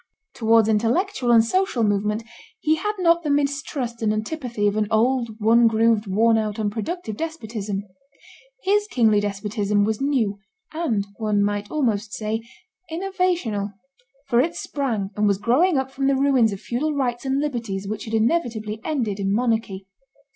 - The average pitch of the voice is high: Yes, high, 230 Hz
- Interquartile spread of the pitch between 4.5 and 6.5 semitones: Yes, average, 4.8 semitones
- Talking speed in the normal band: Yes, average, 155 wpm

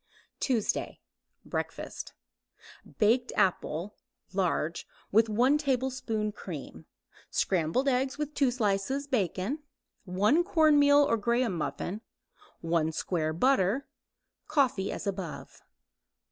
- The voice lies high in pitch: Yes, high, 220 Hz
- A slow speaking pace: Yes, slow, 95 wpm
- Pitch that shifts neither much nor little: No, wide, 6.4 semitones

